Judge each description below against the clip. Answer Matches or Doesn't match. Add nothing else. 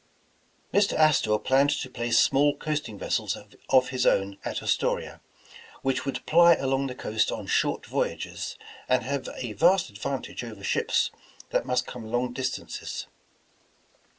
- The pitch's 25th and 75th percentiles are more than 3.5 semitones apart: Doesn't match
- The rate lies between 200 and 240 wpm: Doesn't match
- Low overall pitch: Matches